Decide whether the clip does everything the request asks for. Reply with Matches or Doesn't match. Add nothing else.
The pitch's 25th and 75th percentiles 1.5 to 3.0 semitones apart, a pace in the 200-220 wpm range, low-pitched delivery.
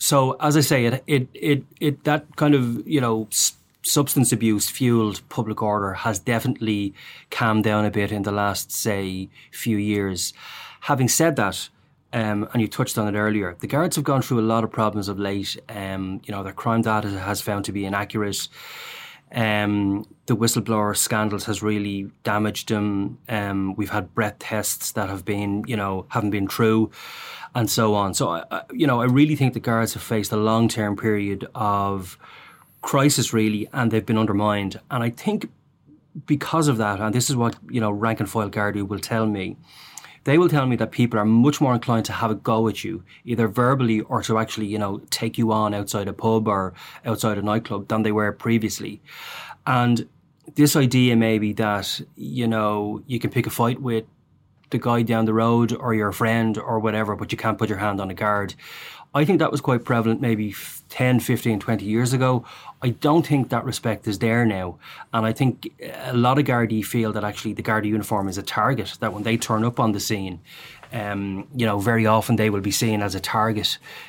Matches